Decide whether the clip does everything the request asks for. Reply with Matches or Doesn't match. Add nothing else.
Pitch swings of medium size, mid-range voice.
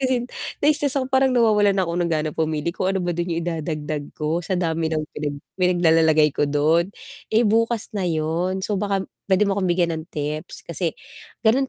Matches